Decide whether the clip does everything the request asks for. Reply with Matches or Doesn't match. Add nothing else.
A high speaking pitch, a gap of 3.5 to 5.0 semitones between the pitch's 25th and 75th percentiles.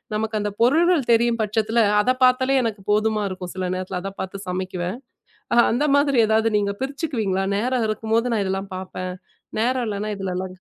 Matches